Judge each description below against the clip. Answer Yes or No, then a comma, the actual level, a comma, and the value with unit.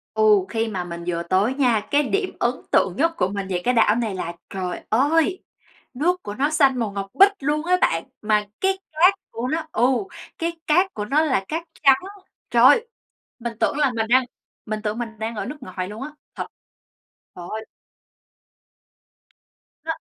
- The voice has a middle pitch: No, high, 240 Hz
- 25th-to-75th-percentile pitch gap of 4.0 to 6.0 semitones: No, wide, 6.7 semitones